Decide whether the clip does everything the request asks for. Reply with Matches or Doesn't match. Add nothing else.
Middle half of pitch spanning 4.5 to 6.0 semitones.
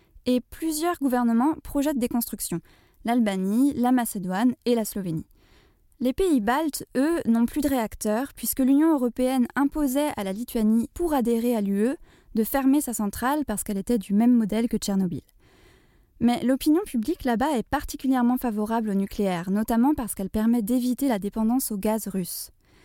Doesn't match